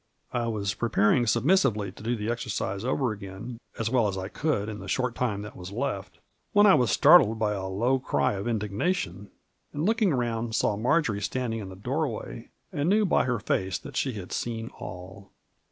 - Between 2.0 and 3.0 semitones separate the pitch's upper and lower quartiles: No, average, 4.2 semitones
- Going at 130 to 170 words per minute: No, average, 195 wpm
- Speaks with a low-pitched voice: Yes, low, 115 Hz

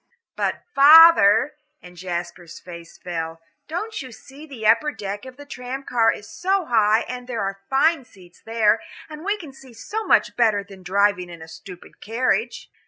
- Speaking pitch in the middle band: No, high, 225 Hz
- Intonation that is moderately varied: No, wide, 6.4 semitones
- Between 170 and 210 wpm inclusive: Yes, average, 175 wpm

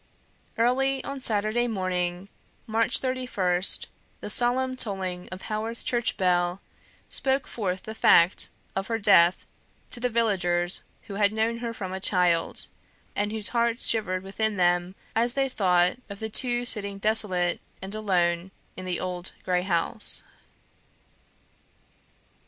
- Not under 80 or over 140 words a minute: Yes, slow, 135 wpm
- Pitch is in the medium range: No, high, 200 Hz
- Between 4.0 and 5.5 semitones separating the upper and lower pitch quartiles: Yes, average, 4.3 semitones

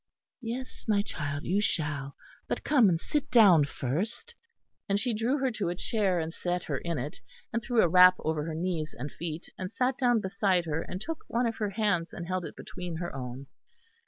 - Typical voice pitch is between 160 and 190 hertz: Yes, medium, 185 Hz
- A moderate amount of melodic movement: No, wide, 5.7 semitones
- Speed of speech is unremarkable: No, fast, 210 wpm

